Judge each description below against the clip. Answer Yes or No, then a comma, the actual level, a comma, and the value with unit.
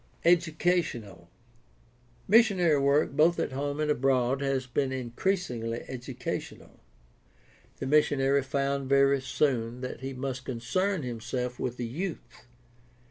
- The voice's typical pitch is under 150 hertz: Yes, low, 135 Hz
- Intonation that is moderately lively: Yes, average, 3.4 semitones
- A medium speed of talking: No, slow, 120 wpm